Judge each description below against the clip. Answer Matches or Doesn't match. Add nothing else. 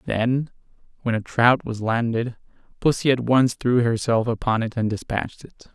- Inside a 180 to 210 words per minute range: Doesn't match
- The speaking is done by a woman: Doesn't match